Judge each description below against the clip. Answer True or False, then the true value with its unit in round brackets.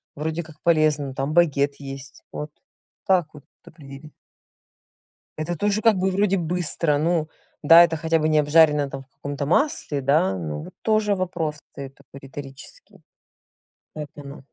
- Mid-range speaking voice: True (150 Hz)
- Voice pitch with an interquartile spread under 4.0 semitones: True (3.5 semitones)